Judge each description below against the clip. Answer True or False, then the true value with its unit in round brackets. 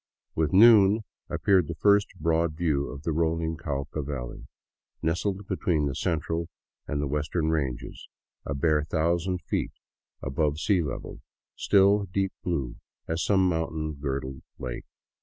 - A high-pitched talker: False (80 Hz)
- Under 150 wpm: True (140 wpm)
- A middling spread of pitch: True (3.7 semitones)